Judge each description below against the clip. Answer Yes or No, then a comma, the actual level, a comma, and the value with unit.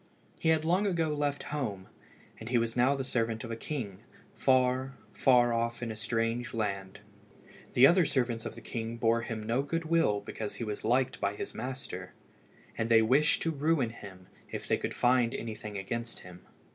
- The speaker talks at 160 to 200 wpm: Yes, average, 190 wpm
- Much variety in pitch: No, average, 3.4 semitones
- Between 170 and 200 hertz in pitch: No, low, 120 Hz